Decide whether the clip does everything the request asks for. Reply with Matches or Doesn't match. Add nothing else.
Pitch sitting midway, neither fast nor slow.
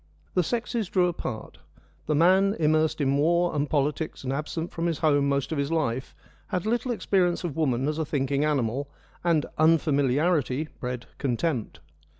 Matches